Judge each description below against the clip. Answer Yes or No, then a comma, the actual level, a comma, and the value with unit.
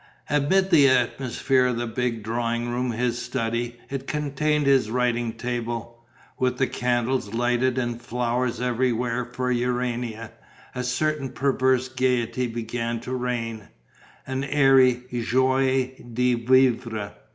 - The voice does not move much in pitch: Yes, narrow, 1.7 semitones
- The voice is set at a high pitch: No, low, 125 Hz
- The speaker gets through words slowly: Yes, slow, 125 wpm